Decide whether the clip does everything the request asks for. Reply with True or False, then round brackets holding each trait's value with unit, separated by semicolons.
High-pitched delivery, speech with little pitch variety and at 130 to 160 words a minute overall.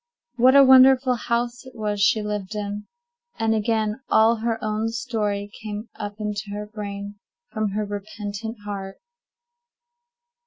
True (215 Hz; 2.0 semitones; 140 wpm)